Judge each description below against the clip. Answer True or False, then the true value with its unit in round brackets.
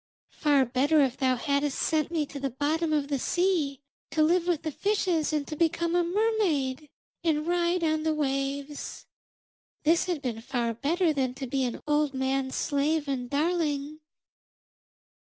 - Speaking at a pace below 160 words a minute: False (165 wpm)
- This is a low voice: False (295 Hz)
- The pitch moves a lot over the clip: False (3.3 semitones)